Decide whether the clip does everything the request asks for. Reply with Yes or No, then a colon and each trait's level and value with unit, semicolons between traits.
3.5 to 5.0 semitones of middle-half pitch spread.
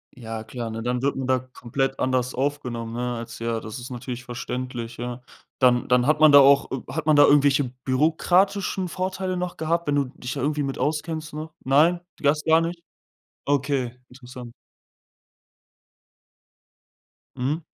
Yes: average, 3.8 semitones